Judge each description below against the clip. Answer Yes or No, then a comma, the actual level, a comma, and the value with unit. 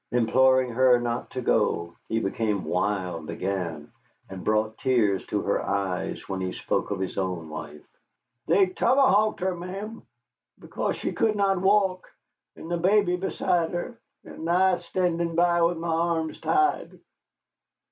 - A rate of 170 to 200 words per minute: No, average, 145 wpm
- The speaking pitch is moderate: Yes, medium, 160 Hz